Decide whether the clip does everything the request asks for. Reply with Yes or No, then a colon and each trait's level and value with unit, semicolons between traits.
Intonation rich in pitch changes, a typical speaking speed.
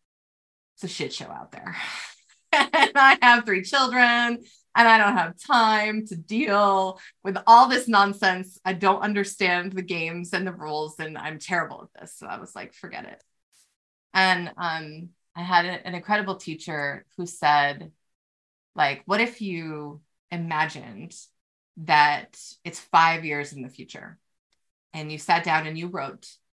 No: average, 4.4 semitones; average, 155 wpm